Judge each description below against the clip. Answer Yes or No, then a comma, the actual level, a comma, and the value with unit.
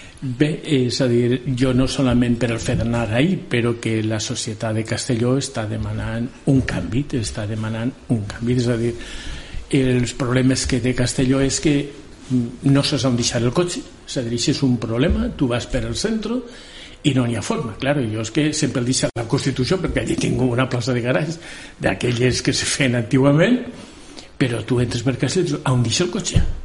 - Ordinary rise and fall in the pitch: Yes, average, 3.1 semitones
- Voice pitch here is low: Yes, low, 130 Hz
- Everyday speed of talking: No, fast, 205 wpm